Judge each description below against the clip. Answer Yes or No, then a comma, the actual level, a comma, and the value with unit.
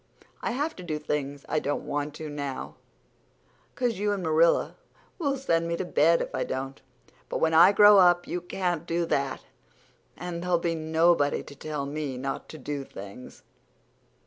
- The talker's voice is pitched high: No, medium, 160 Hz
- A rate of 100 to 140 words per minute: No, average, 170 wpm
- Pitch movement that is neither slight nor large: Yes, average, 3.5 semitones